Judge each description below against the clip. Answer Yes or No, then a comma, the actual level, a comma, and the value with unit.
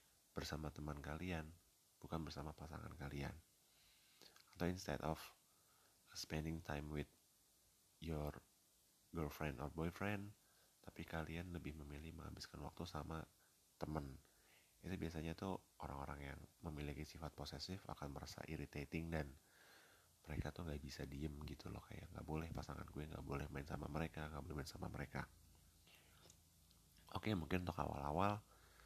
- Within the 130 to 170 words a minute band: Yes, average, 135 wpm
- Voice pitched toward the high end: No, very low, 80 Hz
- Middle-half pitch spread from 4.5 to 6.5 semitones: No, narrow, 2.6 semitones